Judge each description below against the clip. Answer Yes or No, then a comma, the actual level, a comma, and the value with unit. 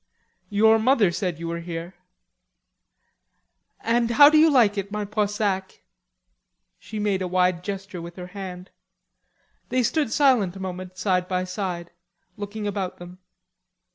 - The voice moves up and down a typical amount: Yes, average, 3.0 semitones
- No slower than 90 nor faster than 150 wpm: Yes, average, 140 wpm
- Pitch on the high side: Yes, high, 195 Hz